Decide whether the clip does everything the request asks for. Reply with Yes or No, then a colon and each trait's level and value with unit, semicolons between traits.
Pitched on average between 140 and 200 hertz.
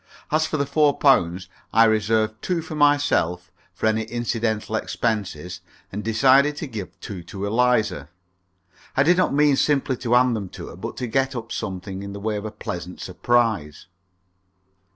No: low, 110 Hz